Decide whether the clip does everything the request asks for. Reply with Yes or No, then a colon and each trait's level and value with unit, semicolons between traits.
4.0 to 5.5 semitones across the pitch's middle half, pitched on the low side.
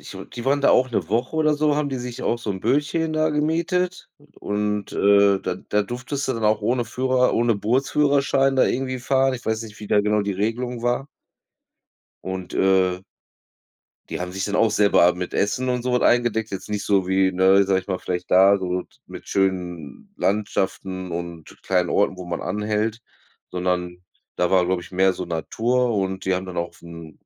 Yes: average, 5.1 semitones; low, 105 Hz